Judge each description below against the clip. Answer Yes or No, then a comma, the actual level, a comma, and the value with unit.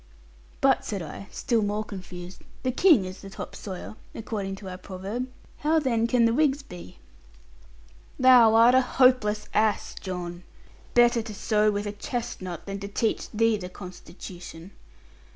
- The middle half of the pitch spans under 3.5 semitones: No, average, 4.1 semitones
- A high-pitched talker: Yes, high, 210 Hz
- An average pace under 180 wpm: Yes, average, 155 wpm